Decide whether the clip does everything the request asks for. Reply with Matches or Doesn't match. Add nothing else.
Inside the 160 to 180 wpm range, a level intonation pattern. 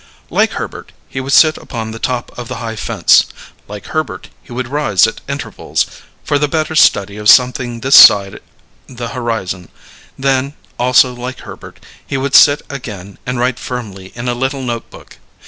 Doesn't match